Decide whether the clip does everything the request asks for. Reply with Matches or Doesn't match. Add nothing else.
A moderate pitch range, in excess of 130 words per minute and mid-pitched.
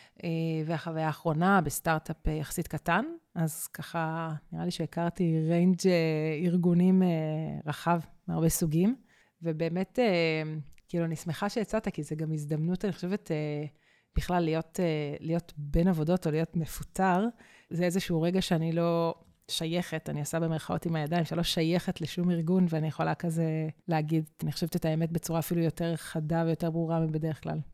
Doesn't match